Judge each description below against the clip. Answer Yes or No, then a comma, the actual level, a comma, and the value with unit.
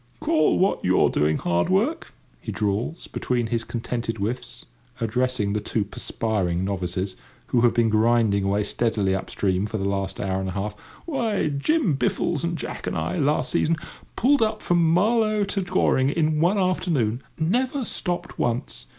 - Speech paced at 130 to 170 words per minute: Yes, average, 165 wpm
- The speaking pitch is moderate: No, low, 120 Hz